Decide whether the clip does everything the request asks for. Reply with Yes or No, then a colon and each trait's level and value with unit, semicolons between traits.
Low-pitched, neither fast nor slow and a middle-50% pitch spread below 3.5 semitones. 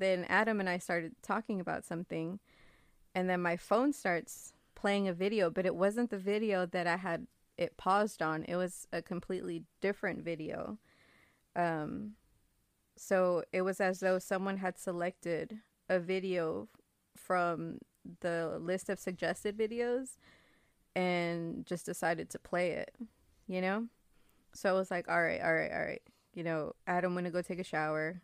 No: medium, 185 Hz; average, 160 wpm; narrow, 2.5 semitones